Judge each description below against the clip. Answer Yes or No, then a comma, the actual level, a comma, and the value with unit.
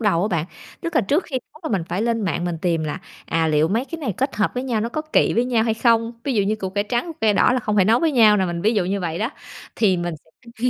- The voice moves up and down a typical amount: Yes, average, 4.7 semitones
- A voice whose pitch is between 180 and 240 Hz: Yes, high, 215 Hz